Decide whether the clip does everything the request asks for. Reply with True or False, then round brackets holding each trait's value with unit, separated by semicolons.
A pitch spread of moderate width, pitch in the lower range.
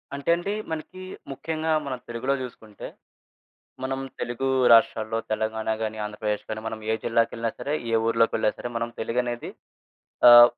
True (3.2 semitones; 115 Hz)